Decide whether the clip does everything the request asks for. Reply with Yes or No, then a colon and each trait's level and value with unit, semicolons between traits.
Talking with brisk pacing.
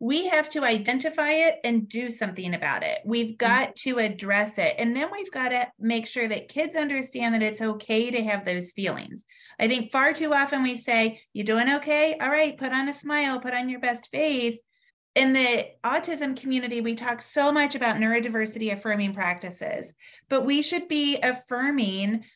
No: average, 190 wpm